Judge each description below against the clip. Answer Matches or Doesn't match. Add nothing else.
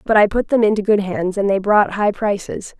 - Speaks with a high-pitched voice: Matches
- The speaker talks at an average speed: Doesn't match